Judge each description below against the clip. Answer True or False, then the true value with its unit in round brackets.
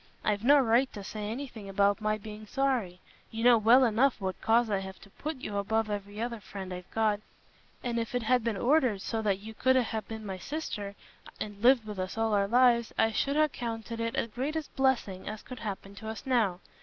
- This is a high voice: True (220 Hz)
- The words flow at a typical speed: False (220 wpm)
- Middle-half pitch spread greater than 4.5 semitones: False (3.3 semitones)